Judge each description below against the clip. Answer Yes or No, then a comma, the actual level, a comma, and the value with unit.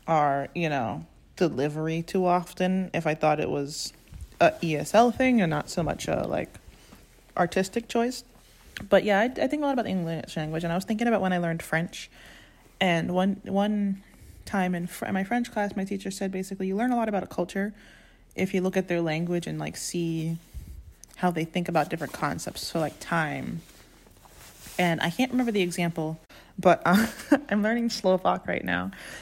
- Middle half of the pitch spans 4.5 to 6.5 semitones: No, average, 3.7 semitones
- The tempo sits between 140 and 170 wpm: No, average, 195 wpm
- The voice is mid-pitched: Yes, medium, 180 Hz